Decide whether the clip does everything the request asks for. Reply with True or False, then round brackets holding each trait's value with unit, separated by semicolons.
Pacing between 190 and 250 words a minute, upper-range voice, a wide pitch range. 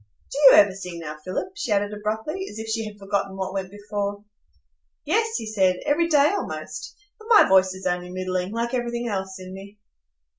False (195 wpm; 205 Hz; 3.9 semitones)